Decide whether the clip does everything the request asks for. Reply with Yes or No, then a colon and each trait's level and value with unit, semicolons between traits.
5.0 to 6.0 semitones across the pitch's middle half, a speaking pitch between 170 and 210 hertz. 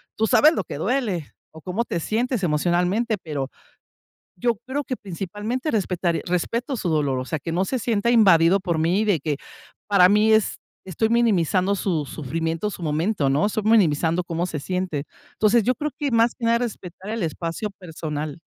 Yes: average, 5.3 semitones; medium, 185 Hz